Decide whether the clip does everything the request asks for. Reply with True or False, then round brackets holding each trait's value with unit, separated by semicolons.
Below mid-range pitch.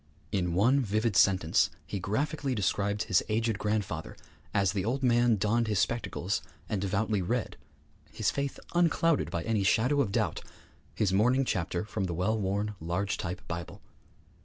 True (105 Hz)